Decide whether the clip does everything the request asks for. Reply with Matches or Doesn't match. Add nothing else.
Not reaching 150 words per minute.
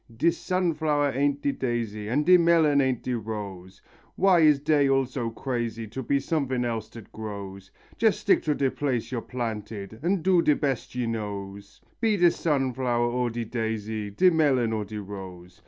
Doesn't match